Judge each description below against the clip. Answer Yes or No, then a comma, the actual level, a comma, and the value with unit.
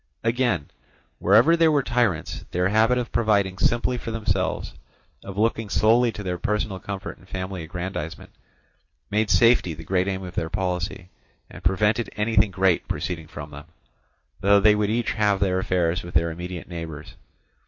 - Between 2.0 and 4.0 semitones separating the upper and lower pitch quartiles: Yes, average, 3.7 semitones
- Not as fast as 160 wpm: No, average, 165 wpm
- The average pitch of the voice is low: Yes, very low, 95 Hz